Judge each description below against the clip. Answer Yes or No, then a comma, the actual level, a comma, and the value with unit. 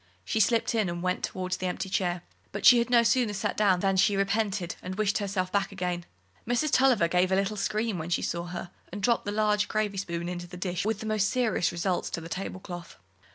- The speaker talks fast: Yes, fast, 230 wpm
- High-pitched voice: Yes, high, 195 Hz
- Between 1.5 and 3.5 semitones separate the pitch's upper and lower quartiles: Yes, average, 3.1 semitones